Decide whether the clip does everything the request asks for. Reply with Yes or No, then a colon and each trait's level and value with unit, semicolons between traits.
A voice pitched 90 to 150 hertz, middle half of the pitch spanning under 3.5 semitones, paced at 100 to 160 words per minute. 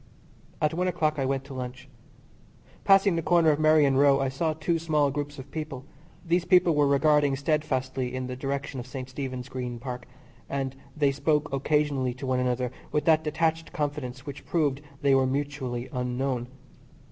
No: medium, 140 Hz; average, 2.9 semitones; average, 175 wpm